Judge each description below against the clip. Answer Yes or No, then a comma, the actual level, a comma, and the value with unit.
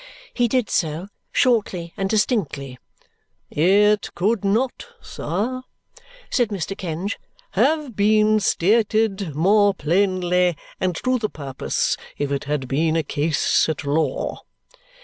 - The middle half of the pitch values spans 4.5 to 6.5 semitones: Yes, average, 5.2 semitones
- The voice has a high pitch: Yes, high, 195 Hz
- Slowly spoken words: Yes, slow, 120 wpm